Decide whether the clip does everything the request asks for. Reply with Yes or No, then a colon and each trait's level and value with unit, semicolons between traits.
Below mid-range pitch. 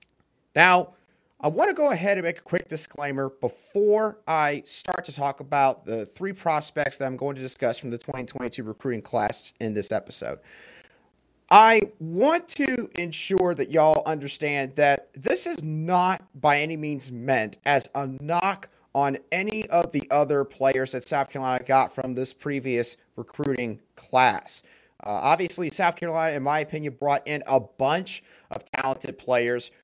No: medium, 145 Hz